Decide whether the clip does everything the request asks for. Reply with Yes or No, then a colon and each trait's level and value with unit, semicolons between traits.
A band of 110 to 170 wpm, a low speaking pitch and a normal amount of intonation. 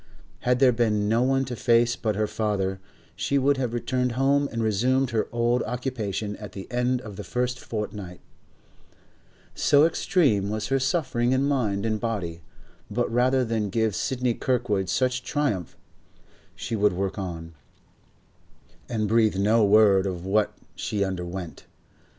Yes: average, 155 wpm; low, 115 Hz; average, 3.7 semitones